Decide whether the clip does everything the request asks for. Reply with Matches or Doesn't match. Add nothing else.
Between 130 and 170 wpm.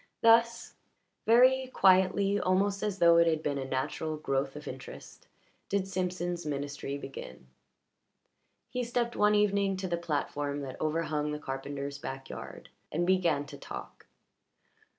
Matches